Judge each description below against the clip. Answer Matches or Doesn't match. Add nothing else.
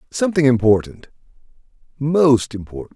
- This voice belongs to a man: Matches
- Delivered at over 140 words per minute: Doesn't match